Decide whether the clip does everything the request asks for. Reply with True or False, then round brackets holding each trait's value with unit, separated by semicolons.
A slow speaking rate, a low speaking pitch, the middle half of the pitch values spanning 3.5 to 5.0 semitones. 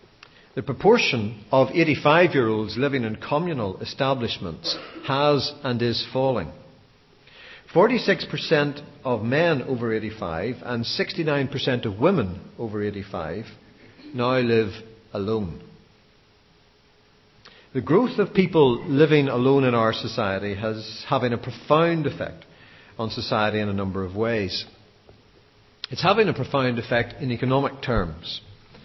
True (120 wpm; 125 Hz; 4.5 semitones)